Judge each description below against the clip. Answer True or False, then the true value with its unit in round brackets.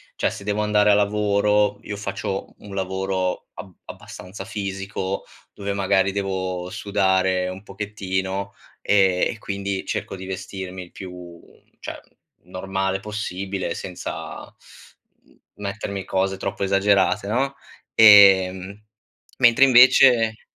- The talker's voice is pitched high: False (95 Hz)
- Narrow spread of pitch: True (1.5 semitones)